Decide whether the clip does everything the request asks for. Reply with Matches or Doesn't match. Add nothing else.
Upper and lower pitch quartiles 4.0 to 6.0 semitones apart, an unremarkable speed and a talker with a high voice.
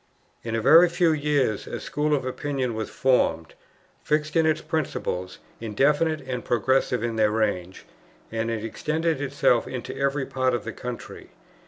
Doesn't match